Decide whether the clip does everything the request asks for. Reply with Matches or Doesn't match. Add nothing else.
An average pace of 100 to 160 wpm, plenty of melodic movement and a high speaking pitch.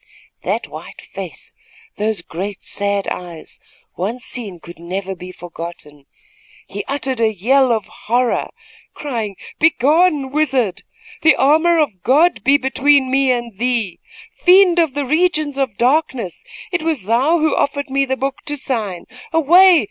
Matches